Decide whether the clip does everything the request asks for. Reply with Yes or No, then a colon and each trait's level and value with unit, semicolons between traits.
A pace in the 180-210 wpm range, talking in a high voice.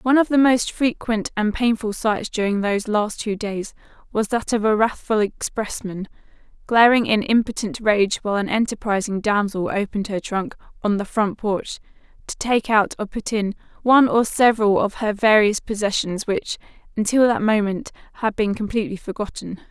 No: average, 165 wpm; high, 215 Hz